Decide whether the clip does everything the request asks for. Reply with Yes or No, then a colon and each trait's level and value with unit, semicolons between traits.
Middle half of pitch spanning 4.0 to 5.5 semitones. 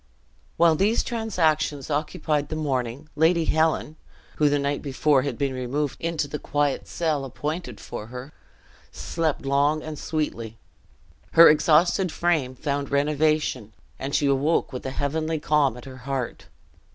No: narrow, 2.5 semitones